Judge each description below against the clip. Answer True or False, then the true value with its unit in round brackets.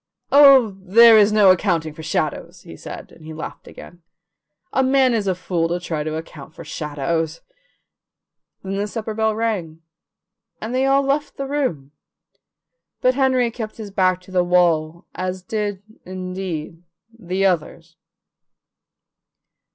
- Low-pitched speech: False (185 Hz)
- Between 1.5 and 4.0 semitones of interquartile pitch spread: False (5.3 semitones)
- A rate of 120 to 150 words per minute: True (145 wpm)